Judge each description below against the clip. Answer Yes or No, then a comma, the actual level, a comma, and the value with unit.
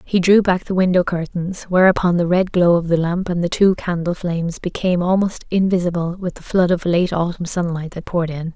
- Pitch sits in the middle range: Yes, medium, 175 Hz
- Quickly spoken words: Yes, fast, 215 wpm